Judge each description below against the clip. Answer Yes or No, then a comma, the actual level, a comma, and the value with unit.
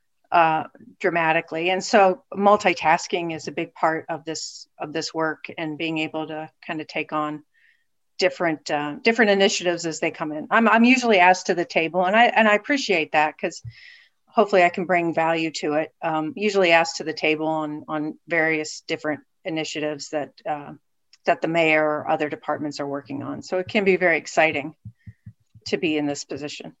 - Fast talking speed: No, average, 190 wpm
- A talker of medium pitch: Yes, medium, 160 Hz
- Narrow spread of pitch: No, average, 3.3 semitones